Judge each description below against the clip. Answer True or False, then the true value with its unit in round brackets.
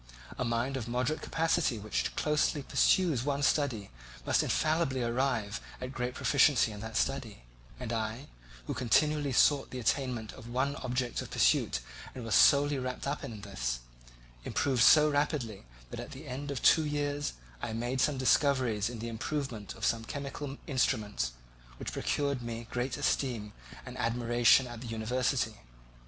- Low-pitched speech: True (125 Hz)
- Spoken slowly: False (160 wpm)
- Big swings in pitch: False (3.6 semitones)